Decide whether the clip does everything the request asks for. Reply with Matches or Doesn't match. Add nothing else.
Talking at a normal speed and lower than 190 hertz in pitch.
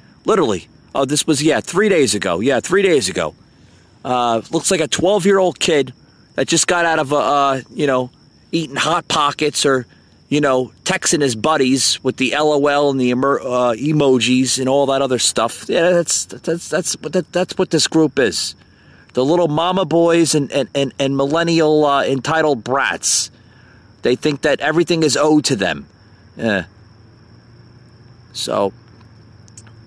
Matches